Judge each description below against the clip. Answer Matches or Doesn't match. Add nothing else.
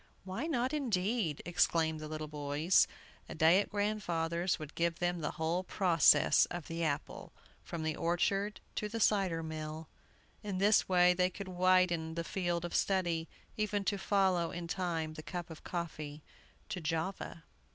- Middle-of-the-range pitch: Matches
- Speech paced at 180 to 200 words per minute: Doesn't match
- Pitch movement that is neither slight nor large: Matches